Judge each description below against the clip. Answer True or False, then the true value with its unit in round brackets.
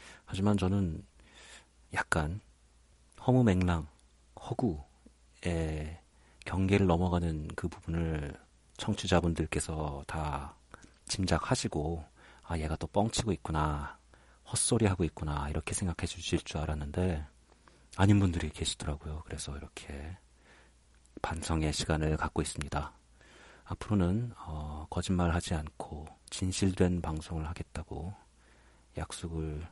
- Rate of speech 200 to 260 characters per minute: True (250 characters per minute)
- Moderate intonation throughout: True (3.5 semitones)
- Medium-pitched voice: False (80 Hz)